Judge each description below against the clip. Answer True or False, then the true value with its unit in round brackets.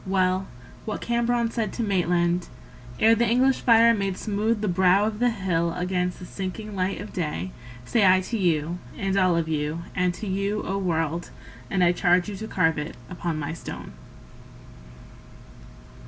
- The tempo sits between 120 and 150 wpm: False (170 wpm)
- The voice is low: False (185 Hz)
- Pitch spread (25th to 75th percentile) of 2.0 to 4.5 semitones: True (3.5 semitones)